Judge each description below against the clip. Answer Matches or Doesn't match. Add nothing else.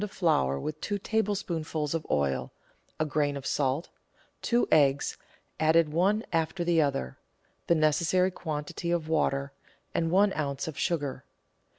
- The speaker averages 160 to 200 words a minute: Doesn't match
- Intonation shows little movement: Doesn't match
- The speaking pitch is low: Doesn't match